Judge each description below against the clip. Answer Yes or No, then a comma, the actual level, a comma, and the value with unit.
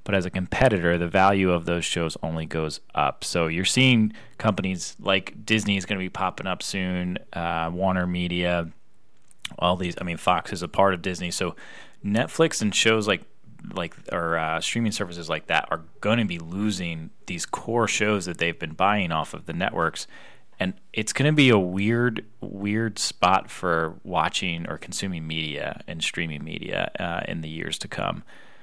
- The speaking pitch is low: Yes, very low, 95 Hz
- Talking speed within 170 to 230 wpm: Yes, average, 185 wpm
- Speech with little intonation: No, average, 3.9 semitones